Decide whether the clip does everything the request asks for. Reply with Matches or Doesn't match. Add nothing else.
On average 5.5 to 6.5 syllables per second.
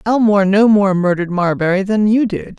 Matches